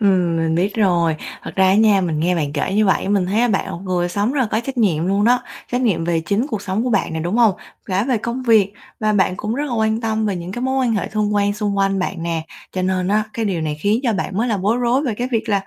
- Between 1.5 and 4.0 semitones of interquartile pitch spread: Yes, average, 3.6 semitones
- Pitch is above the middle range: Yes, high, 205 Hz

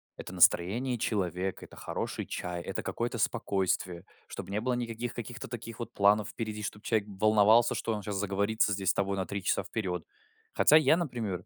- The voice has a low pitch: Yes, low, 105 Hz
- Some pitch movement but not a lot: Yes, average, 3.2 semitones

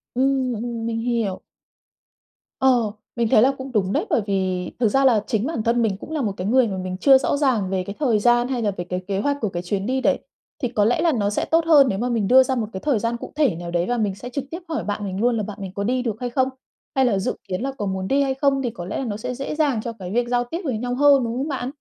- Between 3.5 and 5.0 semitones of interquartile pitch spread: Yes, average, 4.5 semitones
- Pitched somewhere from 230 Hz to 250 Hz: Yes, high, 235 Hz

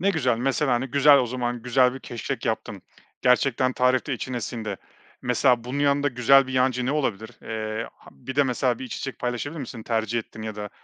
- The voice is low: Yes, low, 125 Hz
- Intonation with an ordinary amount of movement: No, narrow, 2.3 semitones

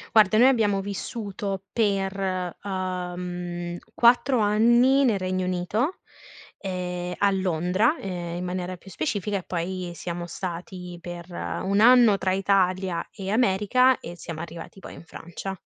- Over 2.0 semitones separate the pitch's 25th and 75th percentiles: Yes, narrow, 2.5 semitones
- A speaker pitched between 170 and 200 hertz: Yes, high, 190 Hz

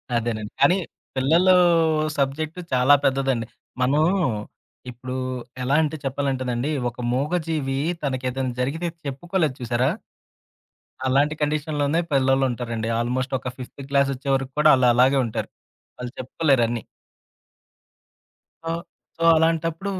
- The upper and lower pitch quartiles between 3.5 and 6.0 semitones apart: No, average, 3.1 semitones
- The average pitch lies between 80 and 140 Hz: Yes, low, 135 Hz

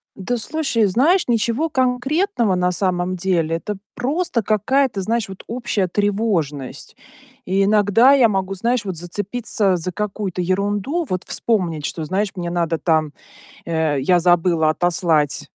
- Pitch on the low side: No, high, 195 Hz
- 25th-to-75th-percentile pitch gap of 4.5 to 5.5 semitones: Yes, average, 4.9 semitones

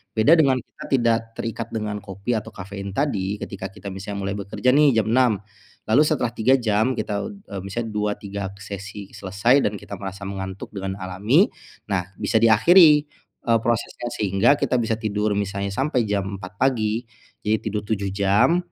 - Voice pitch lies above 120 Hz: No, low, 105 Hz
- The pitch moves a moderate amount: Yes, average, 3.3 semitones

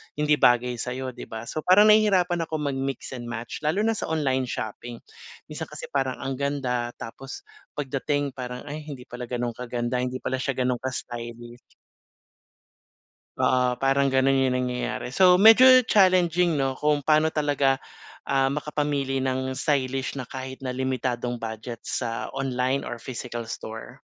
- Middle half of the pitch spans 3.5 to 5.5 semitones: No, average, 2.8 semitones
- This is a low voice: Yes, low, 130 Hz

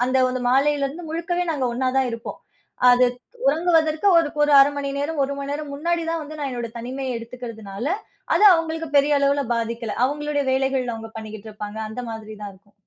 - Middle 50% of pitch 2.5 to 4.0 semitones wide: No, average, 4.5 semitones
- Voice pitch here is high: Yes, very high, 275 Hz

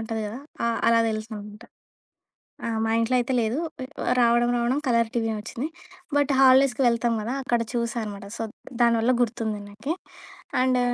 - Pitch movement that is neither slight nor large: No, narrow, 1.7 semitones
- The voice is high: Yes, high, 235 Hz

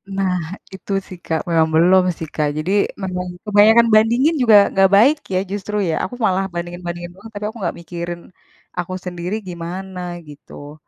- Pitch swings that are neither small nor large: Yes, average, 3.1 semitones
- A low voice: No, medium, 185 Hz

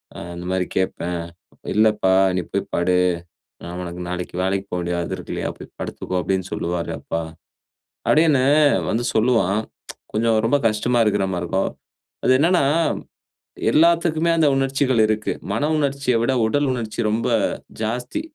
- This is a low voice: Yes, low, 110 Hz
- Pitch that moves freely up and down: Yes, wide, 6.3 semitones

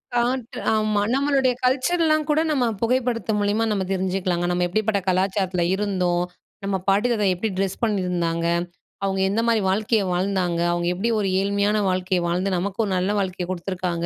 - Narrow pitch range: No, average, 3.7 semitones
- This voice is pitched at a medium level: No, high, 195 Hz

